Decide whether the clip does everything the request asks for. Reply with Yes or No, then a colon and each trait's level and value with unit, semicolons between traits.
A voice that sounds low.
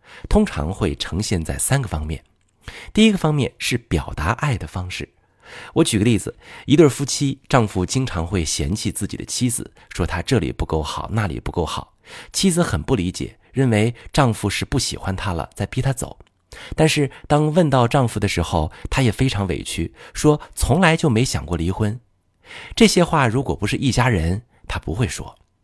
Yes: low, 105 Hz